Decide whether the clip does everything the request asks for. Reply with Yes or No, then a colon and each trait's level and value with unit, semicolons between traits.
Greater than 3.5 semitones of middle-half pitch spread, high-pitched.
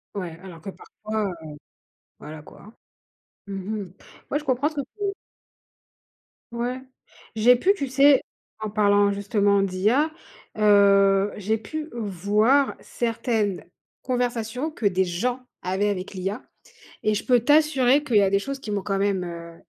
Yes: average, 4.1 semitones; high, 210 Hz